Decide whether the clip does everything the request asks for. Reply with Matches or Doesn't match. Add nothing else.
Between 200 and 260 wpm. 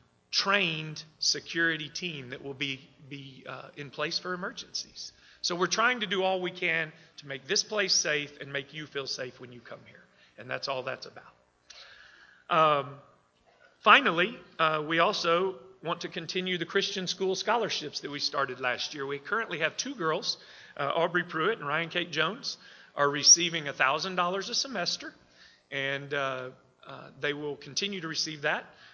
Doesn't match